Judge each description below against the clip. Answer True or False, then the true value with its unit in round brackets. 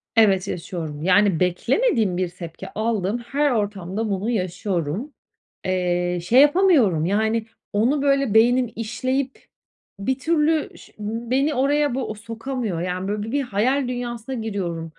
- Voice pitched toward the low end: False (220 Hz)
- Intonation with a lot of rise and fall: True (5.9 semitones)